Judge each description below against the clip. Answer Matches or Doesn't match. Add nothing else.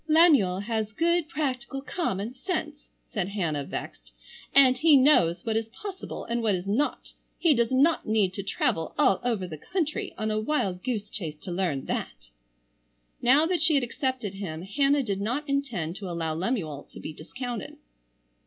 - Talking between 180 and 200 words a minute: Doesn't match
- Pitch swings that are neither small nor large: Doesn't match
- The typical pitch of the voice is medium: Doesn't match